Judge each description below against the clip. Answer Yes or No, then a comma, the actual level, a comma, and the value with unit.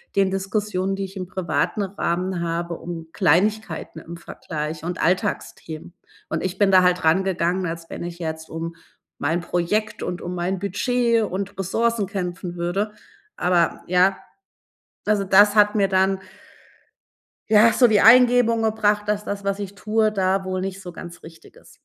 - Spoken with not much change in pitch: No, average, 3.1 semitones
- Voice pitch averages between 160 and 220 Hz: Yes, high, 190 Hz